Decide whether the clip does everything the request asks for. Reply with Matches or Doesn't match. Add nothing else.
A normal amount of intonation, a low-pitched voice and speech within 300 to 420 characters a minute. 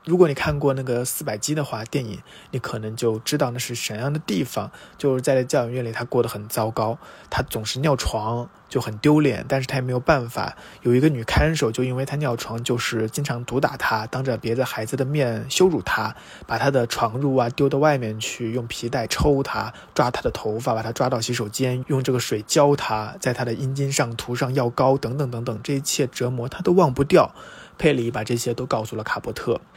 Matches